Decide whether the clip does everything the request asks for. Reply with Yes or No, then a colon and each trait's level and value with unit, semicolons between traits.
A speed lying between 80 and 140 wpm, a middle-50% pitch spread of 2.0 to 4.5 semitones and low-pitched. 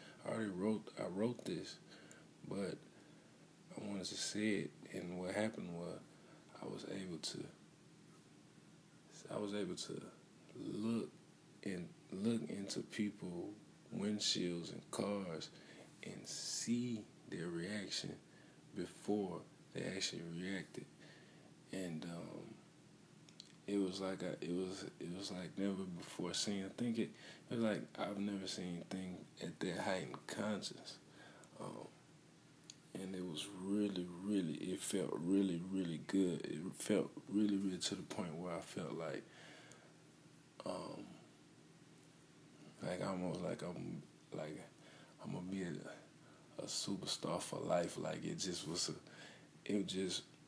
Yes: slow, 135 wpm; narrow, 2.4 semitones; very low, 95 Hz